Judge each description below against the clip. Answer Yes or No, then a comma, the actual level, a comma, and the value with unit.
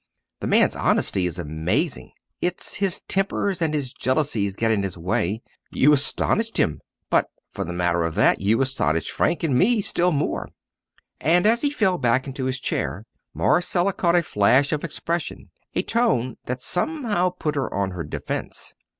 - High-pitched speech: No, medium, 140 Hz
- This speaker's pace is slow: No, average, 170 wpm